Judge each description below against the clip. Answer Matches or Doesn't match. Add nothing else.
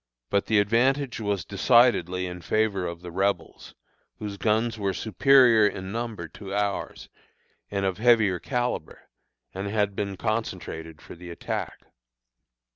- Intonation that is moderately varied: Matches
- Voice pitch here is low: Matches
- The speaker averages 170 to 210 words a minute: Doesn't match